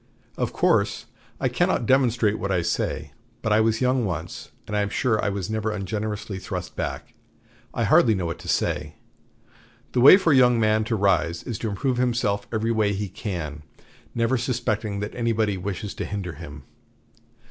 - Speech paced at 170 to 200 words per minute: Yes, average, 180 wpm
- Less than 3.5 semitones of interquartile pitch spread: Yes, average, 3.0 semitones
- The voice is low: Yes, low, 105 Hz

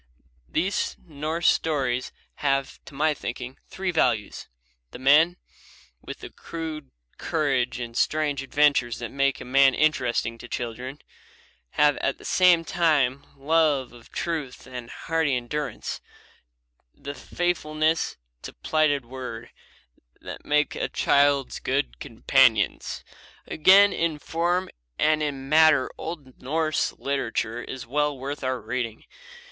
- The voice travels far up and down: No, average, 3.6 semitones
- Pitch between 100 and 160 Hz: Yes, medium, 140 Hz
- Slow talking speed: Yes, slow, 130 wpm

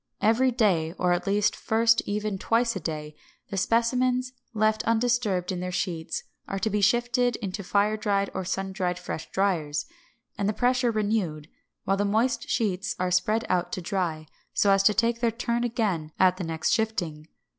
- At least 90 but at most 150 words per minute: No, average, 175 wpm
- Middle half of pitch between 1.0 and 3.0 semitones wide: No, average, 4.0 semitones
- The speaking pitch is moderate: No, high, 205 Hz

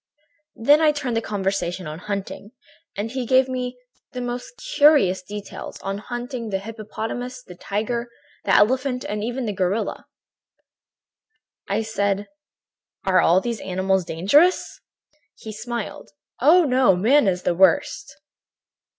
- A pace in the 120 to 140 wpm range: Yes, slow, 135 wpm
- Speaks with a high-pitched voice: Yes, high, 220 Hz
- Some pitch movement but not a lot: Yes, average, 4.4 semitones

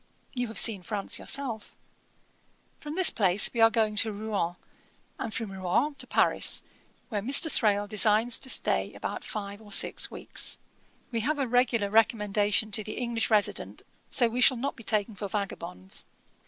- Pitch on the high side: Yes, high, 220 Hz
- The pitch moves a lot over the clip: No, average, 2.8 semitones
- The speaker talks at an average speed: Yes, average, 170 wpm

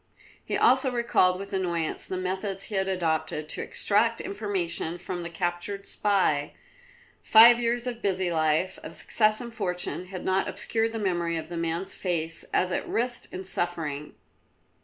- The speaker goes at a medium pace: Yes, average, 160 wpm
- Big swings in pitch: No, average, 3.5 semitones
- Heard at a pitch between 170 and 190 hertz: Yes, medium, 185 Hz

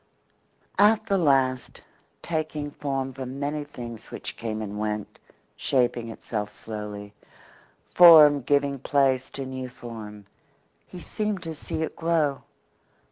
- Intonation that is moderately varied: Yes, average, 4.8 semitones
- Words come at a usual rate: No, slow, 125 wpm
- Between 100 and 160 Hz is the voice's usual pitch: Yes, low, 135 Hz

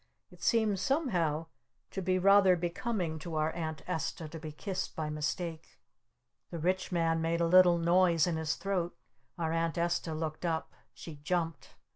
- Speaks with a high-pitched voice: No, medium, 170 Hz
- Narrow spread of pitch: Yes, narrow, 2.3 semitones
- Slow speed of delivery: No, average, 165 wpm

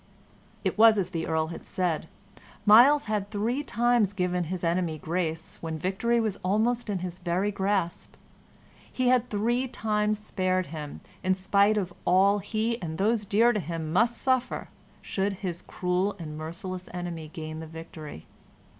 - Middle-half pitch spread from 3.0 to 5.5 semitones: Yes, average, 4.1 semitones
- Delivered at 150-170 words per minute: Yes, average, 160 wpm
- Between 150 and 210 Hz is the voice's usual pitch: Yes, high, 190 Hz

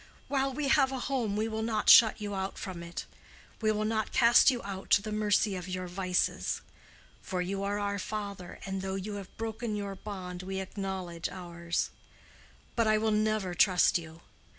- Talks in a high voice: Yes, high, 200 Hz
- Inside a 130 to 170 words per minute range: No, average, 190 wpm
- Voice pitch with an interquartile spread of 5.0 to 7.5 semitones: No, average, 2.8 semitones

